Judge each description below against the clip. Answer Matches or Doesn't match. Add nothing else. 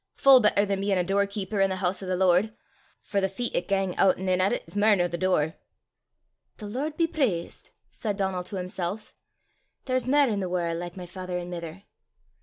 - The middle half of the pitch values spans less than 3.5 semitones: Matches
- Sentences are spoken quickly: Matches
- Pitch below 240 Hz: Matches